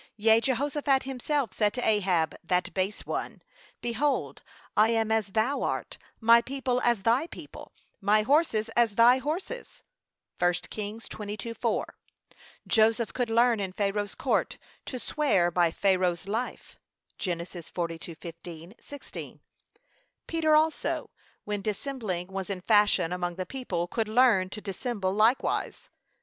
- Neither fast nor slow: No, slow, 130 wpm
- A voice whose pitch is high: Yes, high, 215 Hz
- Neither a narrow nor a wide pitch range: Yes, average, 4.7 semitones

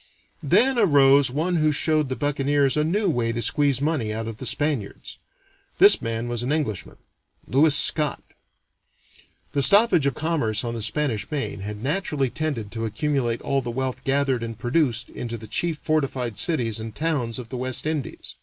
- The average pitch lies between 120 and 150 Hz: Yes, low, 135 Hz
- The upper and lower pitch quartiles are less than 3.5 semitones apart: No, average, 4.6 semitones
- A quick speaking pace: No, average, 175 wpm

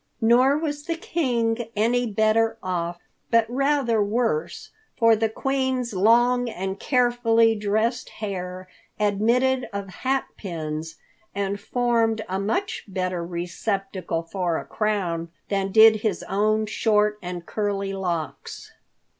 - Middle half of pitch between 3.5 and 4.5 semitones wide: Yes, average, 3.9 semitones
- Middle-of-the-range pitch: No, high, 215 Hz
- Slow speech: Yes, slow, 120 wpm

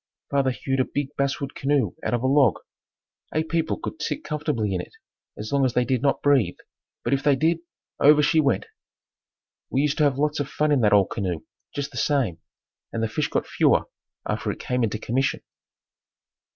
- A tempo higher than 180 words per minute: Yes, average, 200 wpm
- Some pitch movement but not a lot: Yes, average, 3.3 semitones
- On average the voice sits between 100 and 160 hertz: Yes, medium, 140 Hz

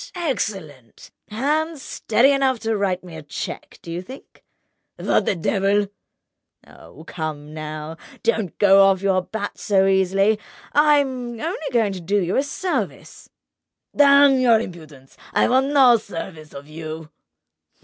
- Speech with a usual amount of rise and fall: No, wide, 7.8 semitones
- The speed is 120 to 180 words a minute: Yes, average, 140 wpm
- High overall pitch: Yes, high, 200 Hz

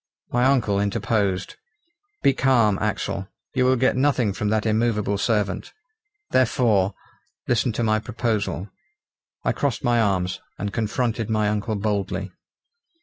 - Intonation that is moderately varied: Yes, average, 3.0 semitones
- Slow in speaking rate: Yes, slow, 130 wpm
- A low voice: Yes, low, 110 Hz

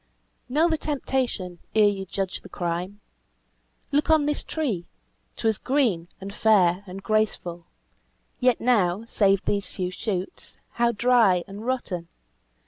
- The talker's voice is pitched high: Yes, high, 205 Hz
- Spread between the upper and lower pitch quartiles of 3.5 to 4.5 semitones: No, average, 5.3 semitones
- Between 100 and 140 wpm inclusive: Yes, slow, 135 wpm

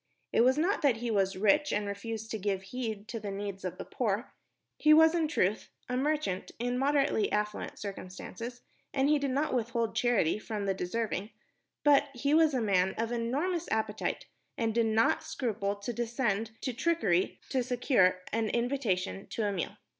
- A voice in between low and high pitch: No, high, 230 Hz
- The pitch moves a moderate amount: Yes, average, 4.5 semitones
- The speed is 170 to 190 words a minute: Yes, average, 180 wpm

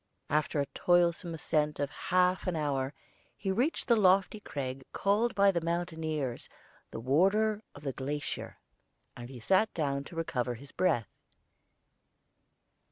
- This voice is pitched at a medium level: Yes, medium, 160 Hz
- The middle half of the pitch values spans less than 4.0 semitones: No, average, 5.1 semitones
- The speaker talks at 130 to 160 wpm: Yes, slow, 135 wpm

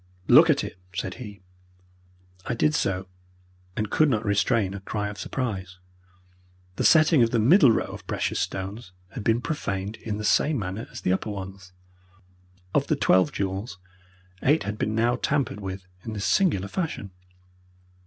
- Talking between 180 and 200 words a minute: No, average, 165 wpm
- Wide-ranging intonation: No, average, 3.9 semitones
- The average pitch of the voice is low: Yes, low, 105 Hz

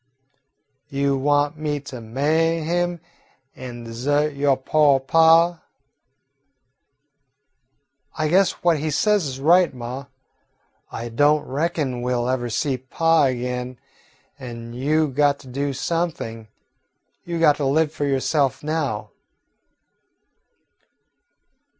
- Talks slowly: Yes, slow, 115 wpm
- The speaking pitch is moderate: Yes, medium, 145 Hz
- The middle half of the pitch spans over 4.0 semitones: No, average, 3.7 semitones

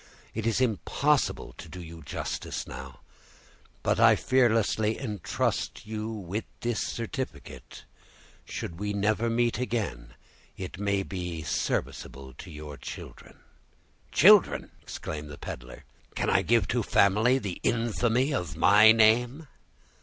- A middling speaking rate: No, slow, 130 wpm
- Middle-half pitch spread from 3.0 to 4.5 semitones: No, average, 5.2 semitones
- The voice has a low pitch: Yes, low, 105 Hz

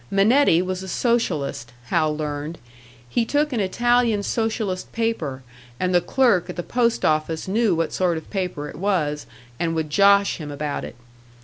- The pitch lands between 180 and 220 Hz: Yes, medium, 185 Hz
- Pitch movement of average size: No, wide, 6.4 semitones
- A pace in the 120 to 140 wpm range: No, average, 170 wpm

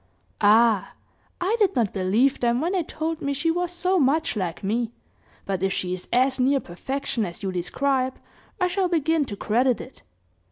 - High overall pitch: Yes, very high, 260 Hz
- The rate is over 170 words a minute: Yes, average, 185 wpm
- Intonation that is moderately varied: No, wide, 7.4 semitones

